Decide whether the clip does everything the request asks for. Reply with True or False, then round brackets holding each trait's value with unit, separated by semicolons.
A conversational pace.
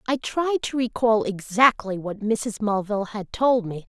True (165 wpm)